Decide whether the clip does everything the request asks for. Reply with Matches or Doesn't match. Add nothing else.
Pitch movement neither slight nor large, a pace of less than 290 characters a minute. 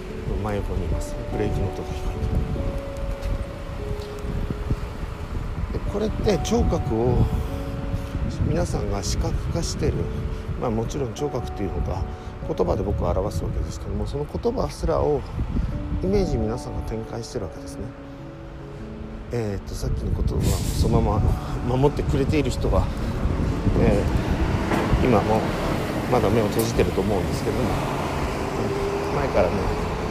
Matches